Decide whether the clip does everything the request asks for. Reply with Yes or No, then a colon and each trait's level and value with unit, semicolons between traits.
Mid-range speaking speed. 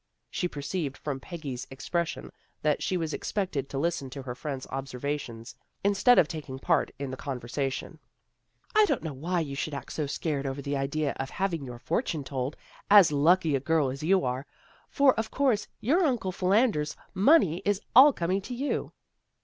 Yes: average, 185 wpm